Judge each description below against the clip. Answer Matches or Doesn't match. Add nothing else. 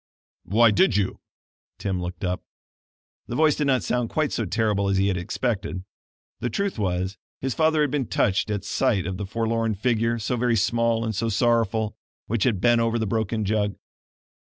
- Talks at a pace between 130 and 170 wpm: Doesn't match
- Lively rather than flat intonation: Doesn't match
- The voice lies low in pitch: Matches